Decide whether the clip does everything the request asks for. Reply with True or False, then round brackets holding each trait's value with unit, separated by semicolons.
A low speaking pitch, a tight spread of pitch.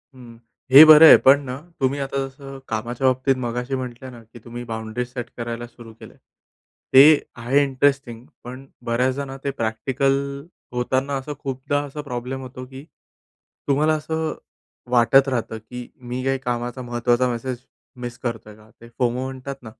True (130 Hz; 2.2 semitones)